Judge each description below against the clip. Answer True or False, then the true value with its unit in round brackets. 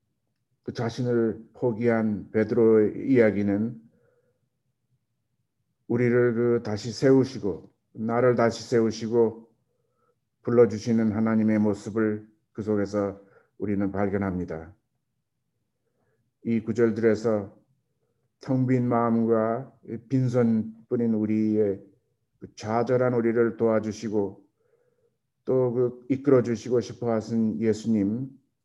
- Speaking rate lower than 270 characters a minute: True (215 characters per minute)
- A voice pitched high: False (115 Hz)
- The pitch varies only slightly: True (2.2 semitones)